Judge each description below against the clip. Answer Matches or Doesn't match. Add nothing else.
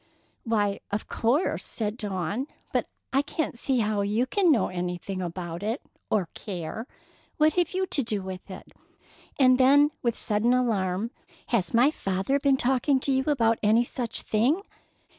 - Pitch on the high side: Matches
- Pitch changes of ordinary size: Matches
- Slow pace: Doesn't match